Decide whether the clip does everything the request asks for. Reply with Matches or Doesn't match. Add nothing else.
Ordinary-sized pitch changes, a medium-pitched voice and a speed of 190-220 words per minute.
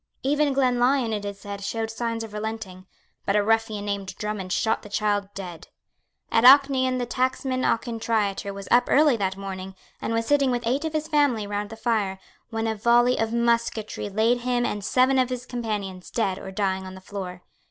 Doesn't match